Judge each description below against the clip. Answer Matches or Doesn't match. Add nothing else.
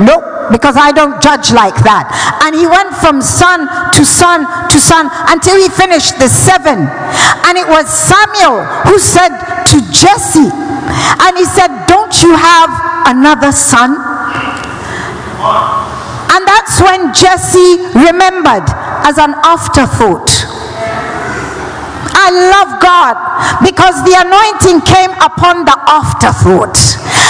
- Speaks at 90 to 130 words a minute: Matches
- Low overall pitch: Doesn't match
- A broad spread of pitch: Doesn't match